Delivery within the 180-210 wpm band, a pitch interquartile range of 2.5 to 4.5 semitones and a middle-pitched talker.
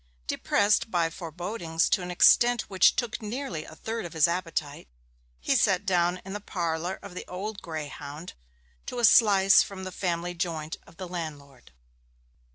No: average, 165 wpm; average, 3.6 semitones; medium, 180 Hz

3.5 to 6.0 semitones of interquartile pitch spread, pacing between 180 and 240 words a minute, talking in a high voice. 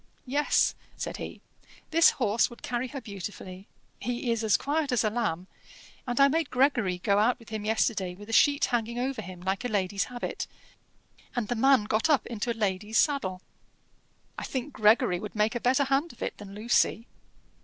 Yes: average, 3.9 semitones; average, 190 wpm; high, 230 Hz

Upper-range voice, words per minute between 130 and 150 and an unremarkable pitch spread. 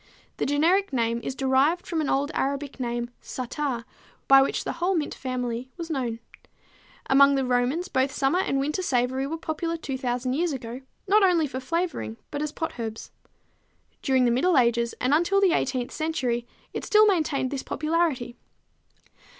No: very high, 270 Hz; average, 165 wpm; average, 4.5 semitones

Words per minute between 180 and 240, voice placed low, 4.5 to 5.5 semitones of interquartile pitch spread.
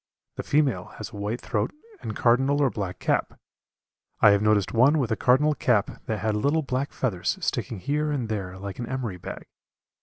Yes: average, 190 wpm; low, 115 Hz; average, 4.9 semitones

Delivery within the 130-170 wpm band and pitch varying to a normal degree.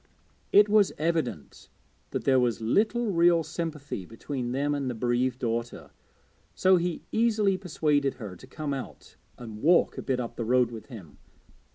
No: average, 165 wpm; wide, 6.0 semitones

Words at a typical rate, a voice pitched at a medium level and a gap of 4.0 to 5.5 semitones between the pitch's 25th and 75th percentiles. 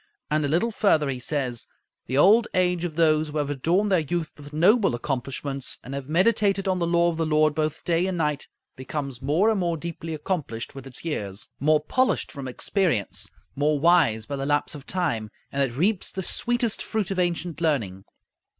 Yes: average, 195 wpm; medium, 155 Hz; average, 4.3 semitones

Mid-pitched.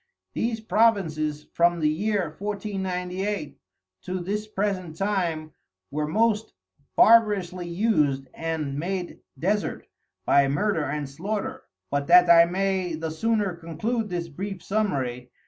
Yes: medium, 180 Hz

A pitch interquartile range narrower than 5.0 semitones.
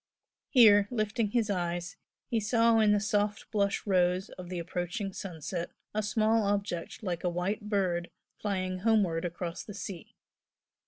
Yes: average, 3.1 semitones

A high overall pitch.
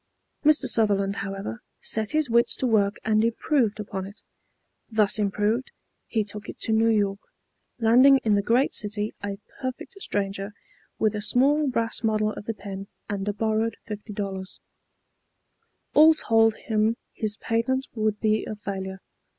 Yes: high, 215 Hz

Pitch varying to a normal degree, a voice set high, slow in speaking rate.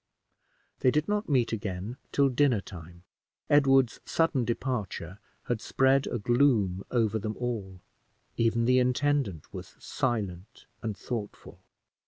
No: average, 4.8 semitones; low, 120 Hz; slow, 125 wpm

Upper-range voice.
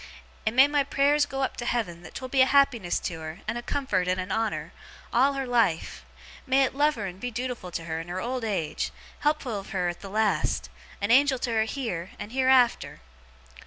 Yes: high, 235 Hz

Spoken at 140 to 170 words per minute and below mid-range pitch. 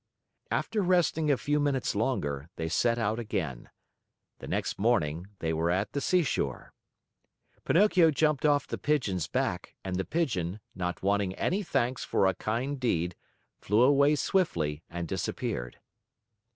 Yes: average, 145 wpm; low, 115 Hz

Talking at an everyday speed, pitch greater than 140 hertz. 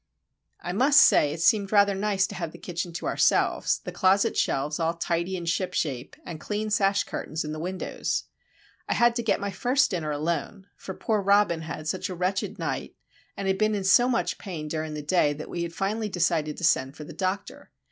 No: fast, 215 wpm; medium, 185 Hz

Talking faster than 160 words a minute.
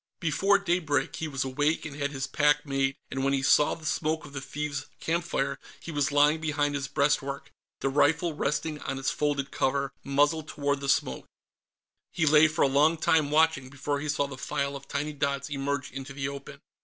Yes: average, 200 wpm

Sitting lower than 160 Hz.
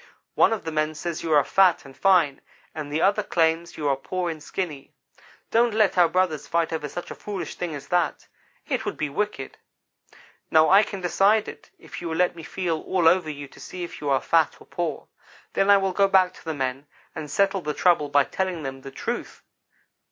No: medium, 170 Hz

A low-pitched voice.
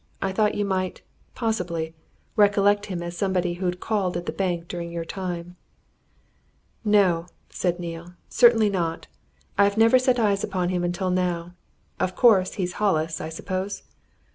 No: medium, 185 Hz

